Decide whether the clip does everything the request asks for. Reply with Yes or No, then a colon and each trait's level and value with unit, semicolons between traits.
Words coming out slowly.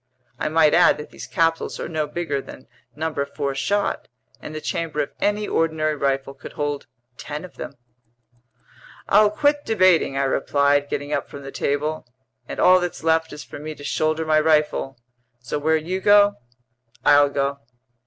No: average, 175 wpm